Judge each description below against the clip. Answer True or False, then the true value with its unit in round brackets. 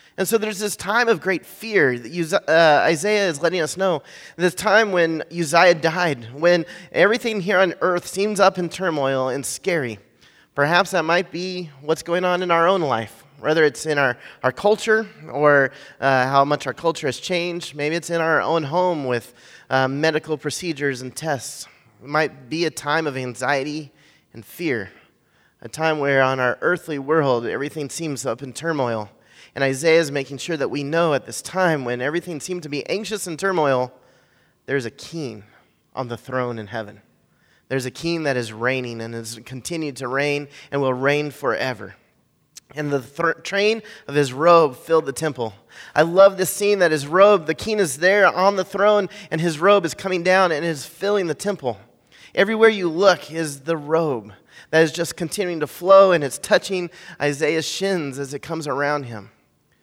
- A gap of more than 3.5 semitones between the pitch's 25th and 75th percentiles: True (4.6 semitones)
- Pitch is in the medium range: True (160 Hz)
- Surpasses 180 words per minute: True (190 wpm)